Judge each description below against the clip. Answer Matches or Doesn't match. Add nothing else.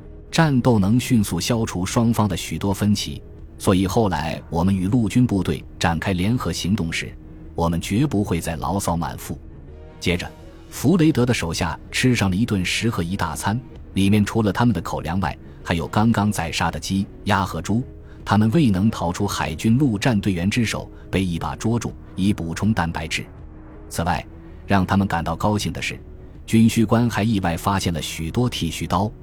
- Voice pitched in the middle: Doesn't match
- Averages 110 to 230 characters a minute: Doesn't match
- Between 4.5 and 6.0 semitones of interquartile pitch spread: Matches